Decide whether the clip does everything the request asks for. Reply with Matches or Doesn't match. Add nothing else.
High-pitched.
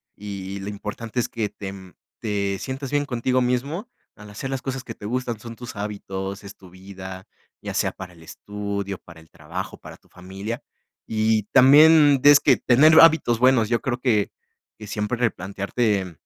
Doesn't match